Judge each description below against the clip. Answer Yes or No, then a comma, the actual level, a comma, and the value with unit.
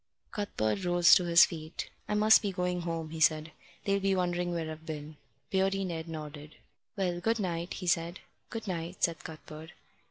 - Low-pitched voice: No, medium, 175 Hz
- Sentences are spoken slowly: No, average, 180 wpm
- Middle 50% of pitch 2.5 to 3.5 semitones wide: Yes, average, 2.8 semitones